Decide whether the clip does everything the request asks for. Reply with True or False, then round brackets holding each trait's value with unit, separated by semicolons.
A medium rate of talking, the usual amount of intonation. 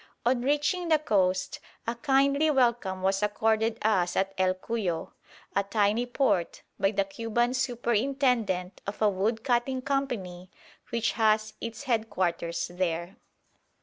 False (130 wpm; 4.4 semitones)